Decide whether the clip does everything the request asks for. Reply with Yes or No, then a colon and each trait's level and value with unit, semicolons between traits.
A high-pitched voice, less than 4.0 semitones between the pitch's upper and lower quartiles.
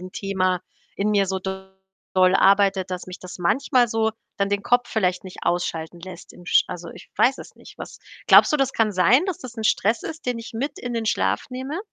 No: high, 200 Hz; average, 4.6 semitones